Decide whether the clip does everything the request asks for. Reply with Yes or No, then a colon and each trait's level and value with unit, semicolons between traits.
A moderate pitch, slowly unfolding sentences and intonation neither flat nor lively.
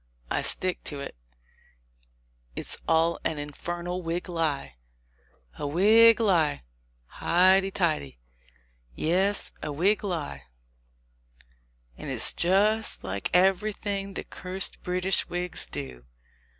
Yes: medium, 175 Hz; slow, 110 wpm; average, 4.7 semitones